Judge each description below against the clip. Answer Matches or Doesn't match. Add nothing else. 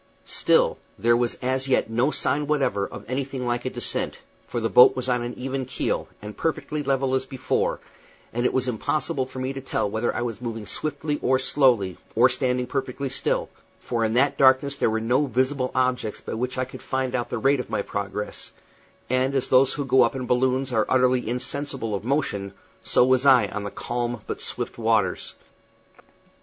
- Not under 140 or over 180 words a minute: Doesn't match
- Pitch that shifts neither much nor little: Doesn't match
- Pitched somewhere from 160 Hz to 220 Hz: Doesn't match